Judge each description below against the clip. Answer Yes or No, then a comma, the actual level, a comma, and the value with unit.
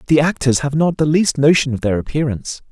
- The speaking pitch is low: No, medium, 145 Hz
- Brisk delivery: Yes, fast, 220 wpm